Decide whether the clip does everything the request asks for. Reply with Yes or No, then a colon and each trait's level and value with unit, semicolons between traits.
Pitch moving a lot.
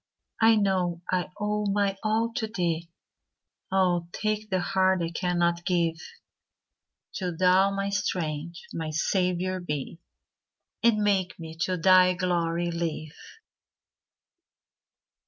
No: narrow, 2.6 semitones